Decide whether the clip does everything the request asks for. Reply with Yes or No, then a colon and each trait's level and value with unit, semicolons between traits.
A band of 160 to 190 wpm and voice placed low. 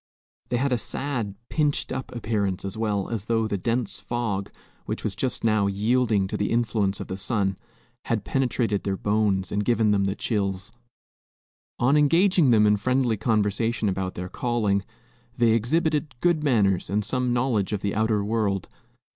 Yes: average, 170 wpm; low, 110 Hz